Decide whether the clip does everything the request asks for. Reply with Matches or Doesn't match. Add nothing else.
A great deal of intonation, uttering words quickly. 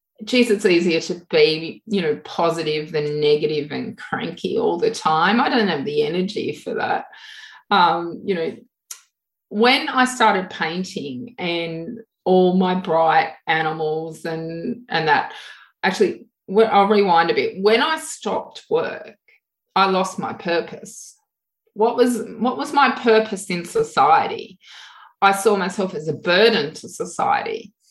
Doesn't match